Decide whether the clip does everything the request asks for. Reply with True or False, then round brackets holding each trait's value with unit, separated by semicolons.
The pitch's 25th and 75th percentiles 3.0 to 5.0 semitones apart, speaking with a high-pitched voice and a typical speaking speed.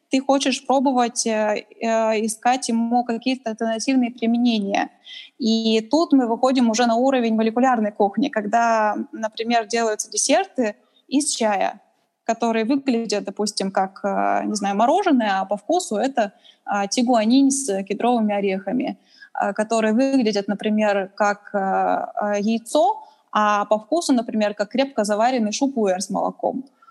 True (3.9 semitones; 230 Hz; 120 wpm)